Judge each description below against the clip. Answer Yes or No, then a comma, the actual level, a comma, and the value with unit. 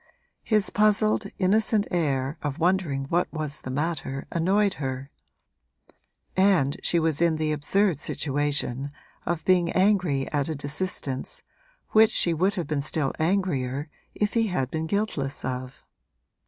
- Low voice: No, medium, 160 Hz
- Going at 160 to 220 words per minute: No, average, 140 wpm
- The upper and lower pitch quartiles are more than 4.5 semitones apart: Yes, average, 5.2 semitones